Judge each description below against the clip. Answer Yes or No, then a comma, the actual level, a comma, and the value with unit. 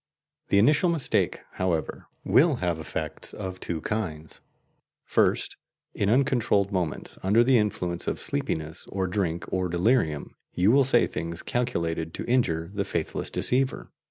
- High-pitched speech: No, very low, 95 Hz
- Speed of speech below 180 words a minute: Yes, average, 140 wpm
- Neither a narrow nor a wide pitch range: No, wide, 6.2 semitones